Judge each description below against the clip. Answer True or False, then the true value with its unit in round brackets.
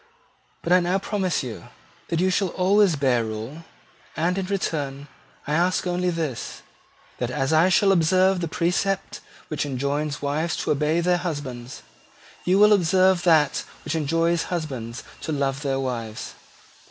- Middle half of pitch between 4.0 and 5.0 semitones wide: True (4.5 semitones)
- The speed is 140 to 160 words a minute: True (155 wpm)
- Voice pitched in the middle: True (160 Hz)